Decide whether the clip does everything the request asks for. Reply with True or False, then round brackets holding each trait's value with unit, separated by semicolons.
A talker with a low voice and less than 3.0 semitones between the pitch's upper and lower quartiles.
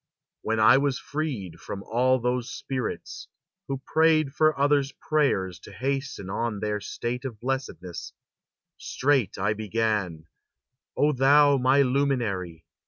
False (125 Hz; 4.9 semitones)